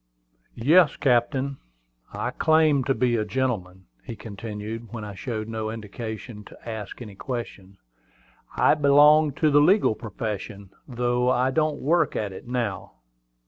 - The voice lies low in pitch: Yes, low, 120 Hz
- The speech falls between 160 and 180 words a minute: No, average, 140 wpm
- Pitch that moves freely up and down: No, average, 4.6 semitones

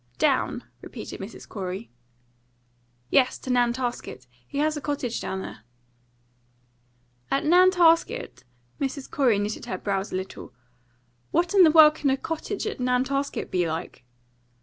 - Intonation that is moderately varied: No, wide, 7.1 semitones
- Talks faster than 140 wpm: No, slow, 135 wpm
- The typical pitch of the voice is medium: No, very high, 260 Hz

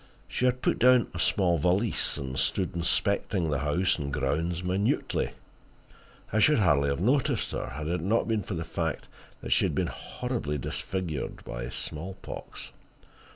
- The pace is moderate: Yes, average, 160 wpm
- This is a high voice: No, very low, 90 Hz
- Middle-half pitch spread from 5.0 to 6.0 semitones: Yes, wide, 5.5 semitones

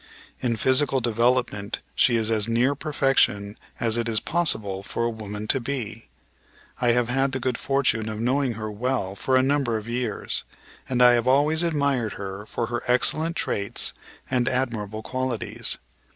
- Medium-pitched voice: No, low, 120 Hz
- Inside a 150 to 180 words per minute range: Yes, average, 165 wpm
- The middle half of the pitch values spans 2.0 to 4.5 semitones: Yes, average, 3.3 semitones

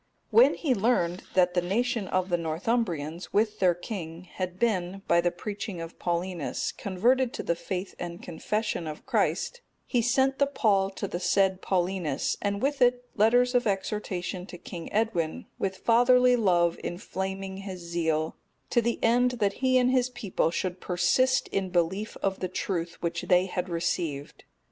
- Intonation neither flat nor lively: Yes, average, 4.8 semitones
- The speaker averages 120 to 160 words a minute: No, average, 170 wpm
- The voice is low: No, high, 190 Hz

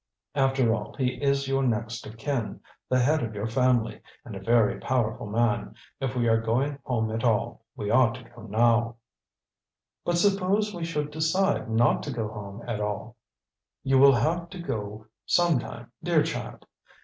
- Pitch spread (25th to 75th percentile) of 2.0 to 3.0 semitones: No, average, 4.2 semitones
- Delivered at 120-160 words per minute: No, average, 175 wpm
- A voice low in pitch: Yes, low, 120 Hz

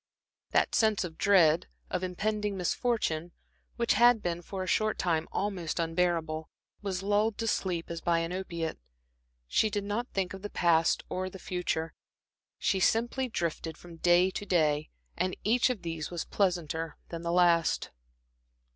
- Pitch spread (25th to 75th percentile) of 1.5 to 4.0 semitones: Yes, average, 3.5 semitones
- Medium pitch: Yes, medium, 180 Hz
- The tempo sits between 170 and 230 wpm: No, average, 160 wpm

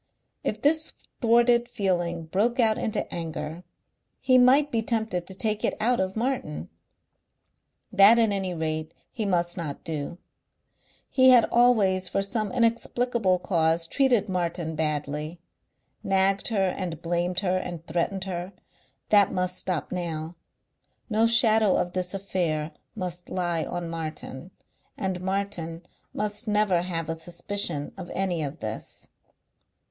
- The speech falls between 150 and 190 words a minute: No, slow, 135 wpm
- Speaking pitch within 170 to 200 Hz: Yes, medium, 185 Hz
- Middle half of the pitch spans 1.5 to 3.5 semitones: No, average, 4.3 semitones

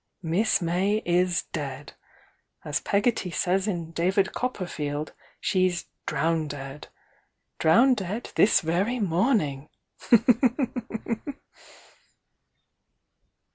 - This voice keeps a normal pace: No, slow, 70 wpm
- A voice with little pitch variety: No, average, 4.2 semitones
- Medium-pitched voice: Yes, medium, 175 Hz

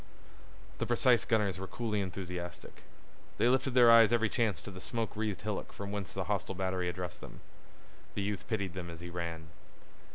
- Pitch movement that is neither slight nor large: Yes, average, 3.6 semitones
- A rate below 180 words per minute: No, average, 185 wpm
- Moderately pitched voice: No, low, 100 Hz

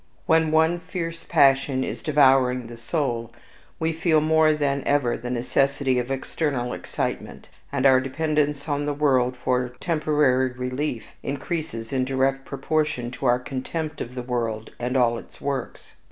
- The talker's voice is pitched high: No, low, 135 Hz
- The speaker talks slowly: No, average, 155 wpm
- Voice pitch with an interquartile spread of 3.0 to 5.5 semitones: Yes, average, 3.3 semitones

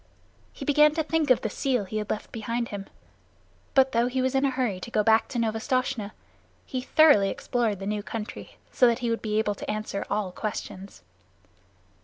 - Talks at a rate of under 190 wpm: No, average, 200 wpm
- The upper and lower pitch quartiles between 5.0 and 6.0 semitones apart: No, average, 3.4 semitones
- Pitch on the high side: Yes, high, 230 Hz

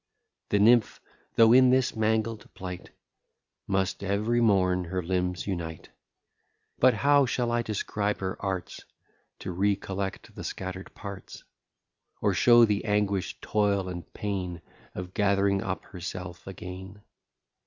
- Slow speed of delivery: Yes, slow, 130 wpm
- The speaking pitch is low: Yes, low, 100 Hz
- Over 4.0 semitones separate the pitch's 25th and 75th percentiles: No, average, 2.8 semitones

